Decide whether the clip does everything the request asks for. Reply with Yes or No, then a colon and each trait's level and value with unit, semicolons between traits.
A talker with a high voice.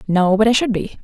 Yes: high, 210 Hz